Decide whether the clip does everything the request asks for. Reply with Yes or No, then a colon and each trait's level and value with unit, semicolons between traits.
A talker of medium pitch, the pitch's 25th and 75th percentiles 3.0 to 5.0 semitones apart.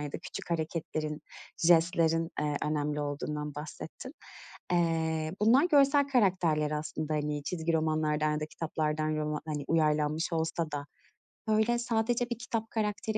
No: medium, 160 Hz; wide, 5.4 semitones